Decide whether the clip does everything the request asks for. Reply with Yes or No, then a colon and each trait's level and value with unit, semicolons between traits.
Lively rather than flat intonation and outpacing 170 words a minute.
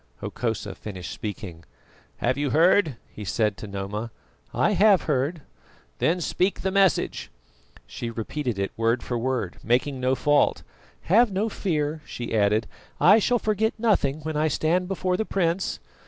No: wide, 8.2 semitones; average, 155 wpm